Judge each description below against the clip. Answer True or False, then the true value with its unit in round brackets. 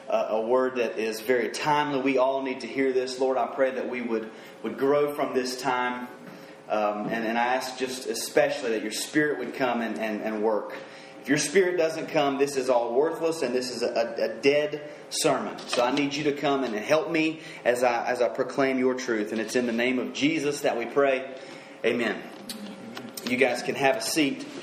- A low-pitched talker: True (130 Hz)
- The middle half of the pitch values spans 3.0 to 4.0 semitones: True (3.4 semitones)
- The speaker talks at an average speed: False (215 wpm)